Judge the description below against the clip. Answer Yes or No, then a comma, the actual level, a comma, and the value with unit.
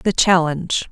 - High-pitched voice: No, medium, 175 Hz